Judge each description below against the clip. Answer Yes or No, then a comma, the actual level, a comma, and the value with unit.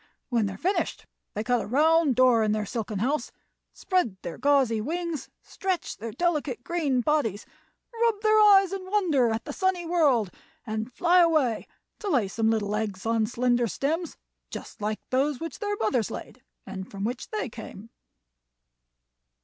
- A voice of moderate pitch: No, very high, 255 Hz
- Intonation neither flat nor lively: No, wide, 7.4 semitones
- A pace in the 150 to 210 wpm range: Yes, average, 165 wpm